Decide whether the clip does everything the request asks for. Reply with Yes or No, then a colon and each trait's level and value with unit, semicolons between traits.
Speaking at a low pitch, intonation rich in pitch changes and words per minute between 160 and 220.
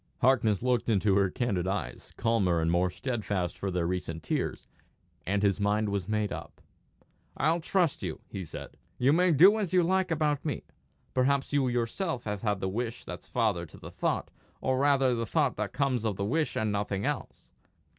Yes: low, 115 Hz; wide, 5.8 semitones; average, 190 wpm